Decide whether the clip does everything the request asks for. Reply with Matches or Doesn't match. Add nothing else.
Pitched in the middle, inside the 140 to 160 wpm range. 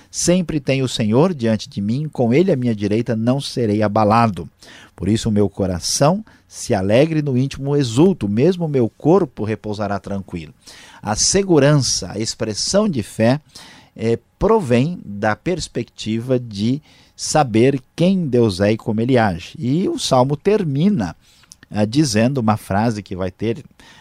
Doesn't match